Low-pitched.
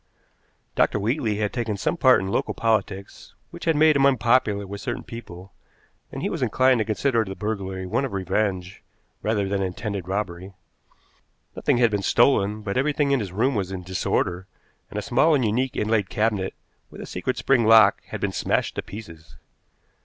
Yes: low, 105 Hz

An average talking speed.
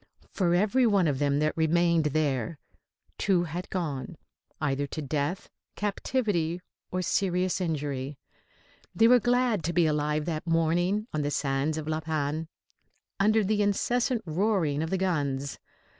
Yes: average, 145 wpm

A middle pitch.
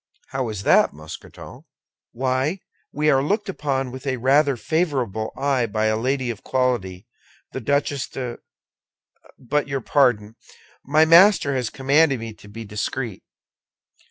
No: low, 130 Hz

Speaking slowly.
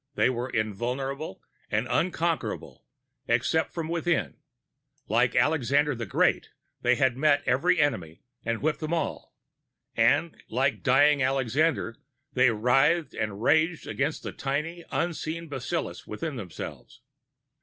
Yes: slow, 125 wpm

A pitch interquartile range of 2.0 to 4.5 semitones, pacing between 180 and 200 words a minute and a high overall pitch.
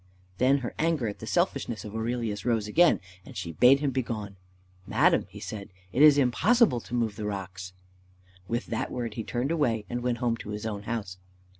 No: average, 3.4 semitones; average, 195 wpm; low, 115 Hz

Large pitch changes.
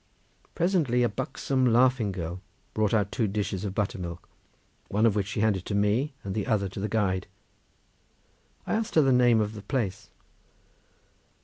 No: average, 3.8 semitones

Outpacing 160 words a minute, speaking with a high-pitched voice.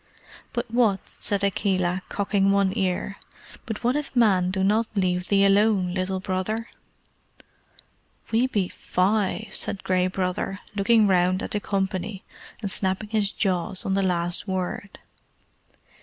No: average, 140 wpm; high, 195 Hz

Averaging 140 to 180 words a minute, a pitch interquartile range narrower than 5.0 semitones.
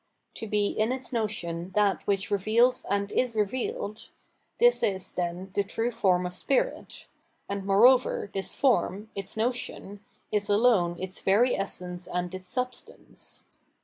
Yes: average, 145 wpm; average, 3.7 semitones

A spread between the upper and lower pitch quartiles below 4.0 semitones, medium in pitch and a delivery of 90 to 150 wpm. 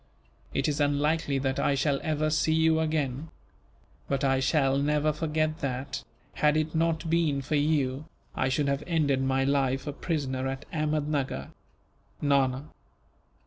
Yes: narrow, 2.4 semitones; medium, 145 Hz; average, 145 wpm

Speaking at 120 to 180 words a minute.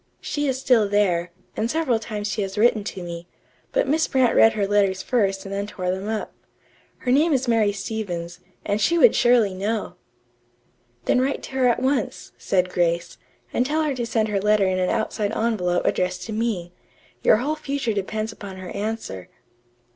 No: average, 190 wpm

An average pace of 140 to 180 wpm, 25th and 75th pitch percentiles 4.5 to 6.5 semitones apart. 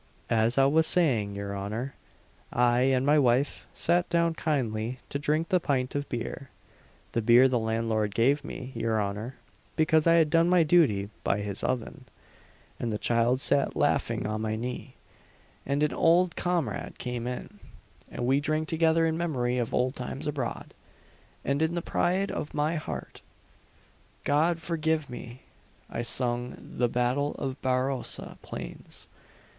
Yes: average, 155 wpm; average, 5.0 semitones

